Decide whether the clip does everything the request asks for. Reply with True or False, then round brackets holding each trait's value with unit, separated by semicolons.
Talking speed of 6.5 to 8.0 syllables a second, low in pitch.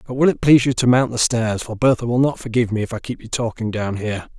True (6.7 syllables/s; 120 Hz)